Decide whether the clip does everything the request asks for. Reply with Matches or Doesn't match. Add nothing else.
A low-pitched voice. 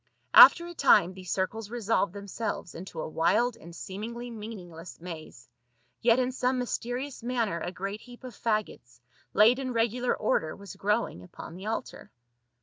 Doesn't match